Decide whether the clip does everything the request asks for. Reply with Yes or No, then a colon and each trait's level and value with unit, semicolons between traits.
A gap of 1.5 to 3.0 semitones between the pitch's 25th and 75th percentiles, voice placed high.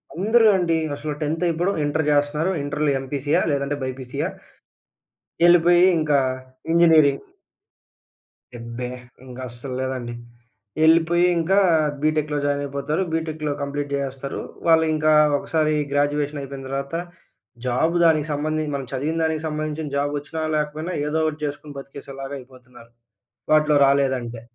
No: narrow, 2.4 semitones; medium, 150 Hz